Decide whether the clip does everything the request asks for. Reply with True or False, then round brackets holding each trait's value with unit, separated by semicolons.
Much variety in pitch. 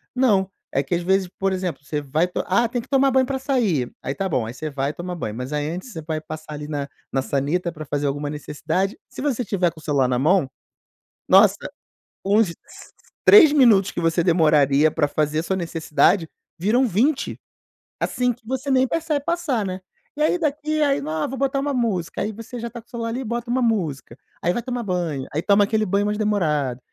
True (7.9 semitones)